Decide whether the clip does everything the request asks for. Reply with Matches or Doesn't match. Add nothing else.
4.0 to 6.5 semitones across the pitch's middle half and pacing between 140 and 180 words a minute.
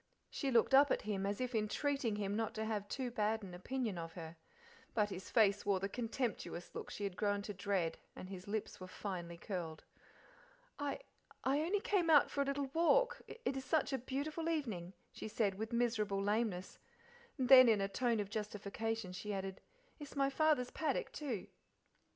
Doesn't match